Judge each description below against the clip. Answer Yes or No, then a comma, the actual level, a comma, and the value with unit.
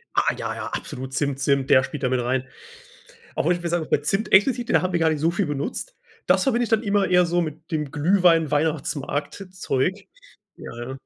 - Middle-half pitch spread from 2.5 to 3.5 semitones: No, average, 4.8 semitones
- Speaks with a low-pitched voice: No, medium, 160 Hz